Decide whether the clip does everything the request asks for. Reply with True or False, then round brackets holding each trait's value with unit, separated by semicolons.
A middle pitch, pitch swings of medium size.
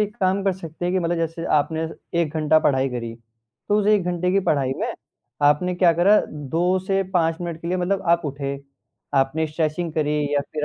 True (165 Hz; 3.2 semitones)